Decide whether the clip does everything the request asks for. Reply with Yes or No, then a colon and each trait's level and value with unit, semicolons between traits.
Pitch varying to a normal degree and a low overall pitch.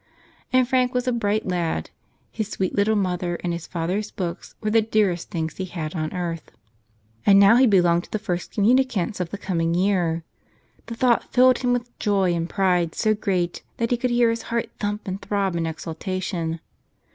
No: average, 4.5 semitones; high, 195 Hz